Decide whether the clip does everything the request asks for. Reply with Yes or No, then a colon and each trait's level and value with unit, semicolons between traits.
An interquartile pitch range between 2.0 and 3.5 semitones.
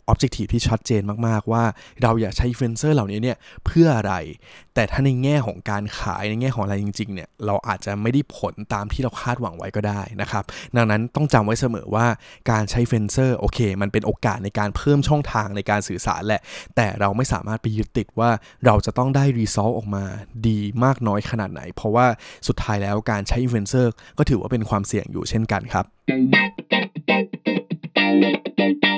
Yes: average, 3.0 semitones